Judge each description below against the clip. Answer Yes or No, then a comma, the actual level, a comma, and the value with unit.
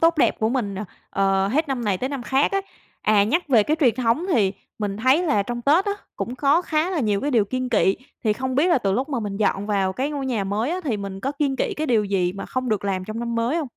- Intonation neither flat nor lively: No, wide, 5.7 semitones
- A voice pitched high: Yes, high, 240 Hz